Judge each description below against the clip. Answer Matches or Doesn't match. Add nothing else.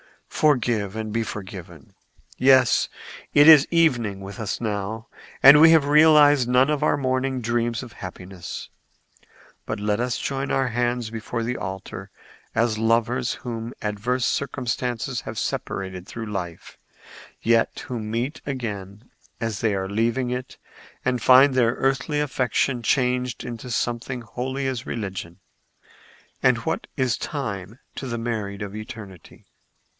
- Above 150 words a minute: Doesn't match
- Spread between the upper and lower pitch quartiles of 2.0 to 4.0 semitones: Matches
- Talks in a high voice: Doesn't match